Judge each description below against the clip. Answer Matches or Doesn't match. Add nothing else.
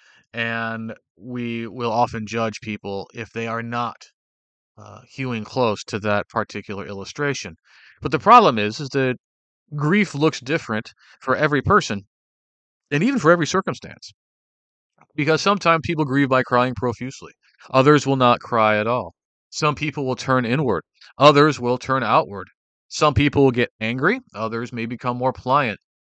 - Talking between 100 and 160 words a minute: Matches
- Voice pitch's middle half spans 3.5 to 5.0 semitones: Matches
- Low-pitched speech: Matches